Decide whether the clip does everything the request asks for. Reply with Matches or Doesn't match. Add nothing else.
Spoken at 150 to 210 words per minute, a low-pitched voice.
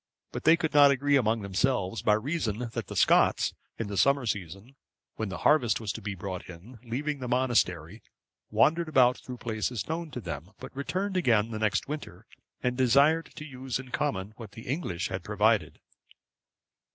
Matches